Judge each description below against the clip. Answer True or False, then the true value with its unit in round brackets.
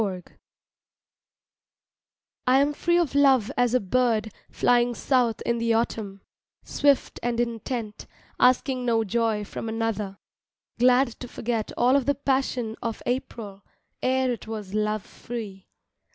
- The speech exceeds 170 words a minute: False (140 wpm)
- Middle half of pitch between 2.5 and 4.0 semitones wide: True (2.8 semitones)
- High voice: True (235 Hz)